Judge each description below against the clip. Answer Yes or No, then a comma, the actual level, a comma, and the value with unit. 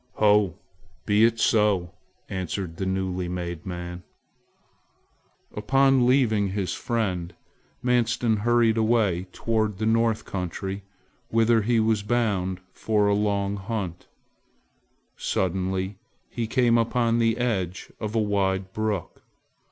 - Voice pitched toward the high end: No, low, 105 Hz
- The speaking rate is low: Yes, slow, 115 wpm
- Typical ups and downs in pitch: Yes, average, 3.4 semitones